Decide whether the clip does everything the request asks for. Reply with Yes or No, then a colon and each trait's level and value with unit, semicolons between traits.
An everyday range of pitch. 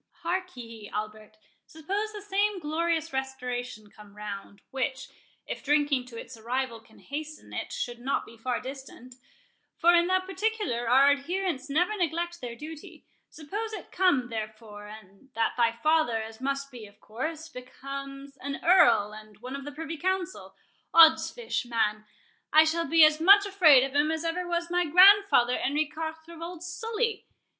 No: wide, 6.1 semitones